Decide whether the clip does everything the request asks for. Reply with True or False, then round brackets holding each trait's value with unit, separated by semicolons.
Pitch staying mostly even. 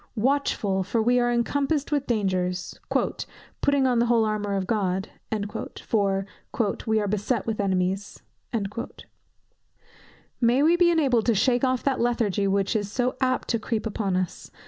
False (4.2 semitones)